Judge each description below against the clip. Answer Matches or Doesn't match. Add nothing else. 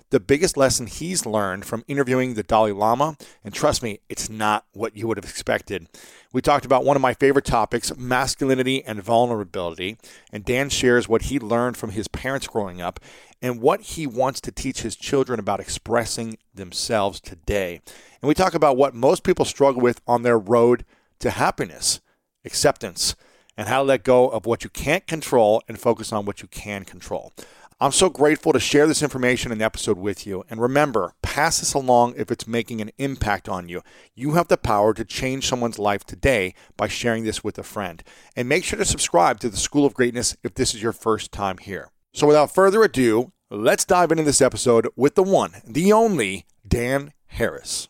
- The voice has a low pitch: Matches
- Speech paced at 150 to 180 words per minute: Doesn't match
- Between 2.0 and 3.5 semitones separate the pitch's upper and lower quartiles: Doesn't match